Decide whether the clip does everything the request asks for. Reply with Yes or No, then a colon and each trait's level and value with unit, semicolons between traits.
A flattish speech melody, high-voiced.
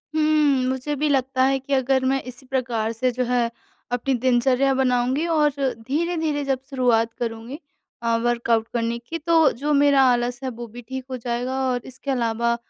Yes: narrow, 2.3 semitones; very high, 255 Hz